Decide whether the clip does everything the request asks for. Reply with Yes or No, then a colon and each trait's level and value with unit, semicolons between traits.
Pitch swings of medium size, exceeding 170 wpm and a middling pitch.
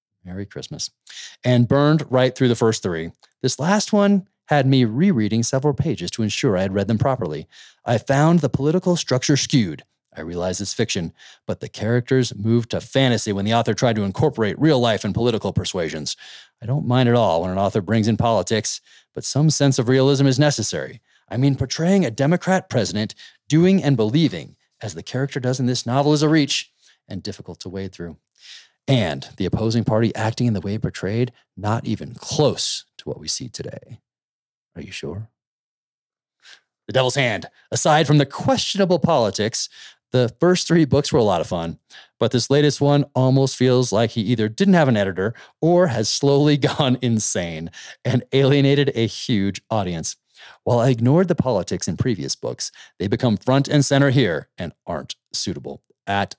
No: average, 4.6 semitones; average, 180 wpm; low, 125 Hz